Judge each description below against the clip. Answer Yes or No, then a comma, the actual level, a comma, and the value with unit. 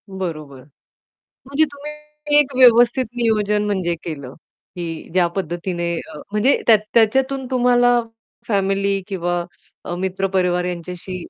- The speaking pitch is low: No, high, 195 Hz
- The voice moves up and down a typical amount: No, wide, 5.7 semitones